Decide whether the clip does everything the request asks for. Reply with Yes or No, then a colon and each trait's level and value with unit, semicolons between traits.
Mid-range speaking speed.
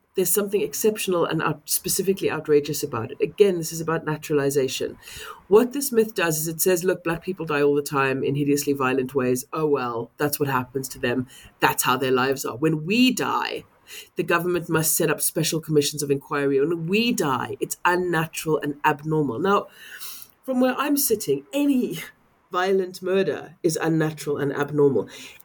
Yes: average, 175 wpm